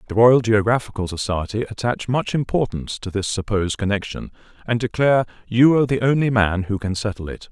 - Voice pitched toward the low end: Yes, low, 110 Hz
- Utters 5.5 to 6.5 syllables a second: Yes, 6.0 syllables/s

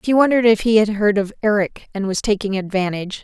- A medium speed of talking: No, fast, 225 wpm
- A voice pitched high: Yes, high, 205 Hz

